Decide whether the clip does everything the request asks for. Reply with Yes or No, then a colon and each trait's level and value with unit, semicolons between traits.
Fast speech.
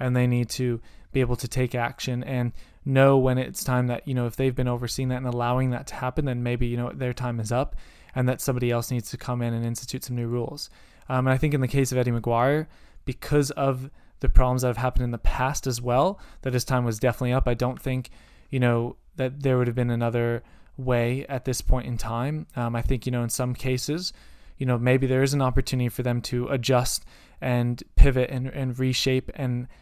Yes: fast, 235 wpm